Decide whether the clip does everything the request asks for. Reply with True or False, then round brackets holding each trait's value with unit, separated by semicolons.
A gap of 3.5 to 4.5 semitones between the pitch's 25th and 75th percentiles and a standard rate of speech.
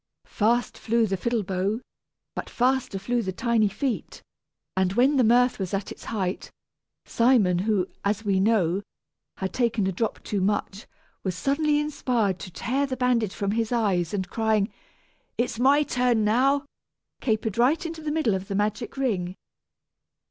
True (4.2 semitones; 165 wpm)